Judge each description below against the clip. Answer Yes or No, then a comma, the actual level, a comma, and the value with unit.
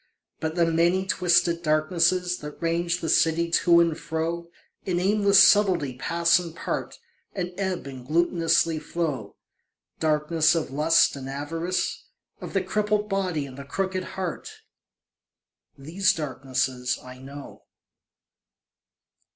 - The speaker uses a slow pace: Yes, slow, 125 wpm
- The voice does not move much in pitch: No, average, 3.1 semitones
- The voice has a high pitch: No, medium, 165 Hz